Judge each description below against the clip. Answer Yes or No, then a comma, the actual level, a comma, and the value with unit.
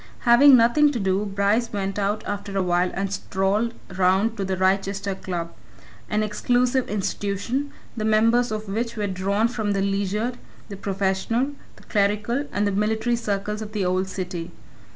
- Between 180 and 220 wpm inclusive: No, average, 165 wpm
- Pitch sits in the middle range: No, high, 205 Hz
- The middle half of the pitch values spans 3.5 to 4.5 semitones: No, average, 2.8 semitones